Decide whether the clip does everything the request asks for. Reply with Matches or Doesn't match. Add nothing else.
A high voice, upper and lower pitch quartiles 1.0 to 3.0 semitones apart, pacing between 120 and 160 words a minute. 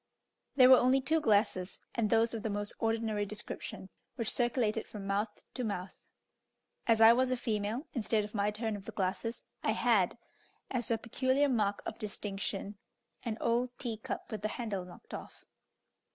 Doesn't match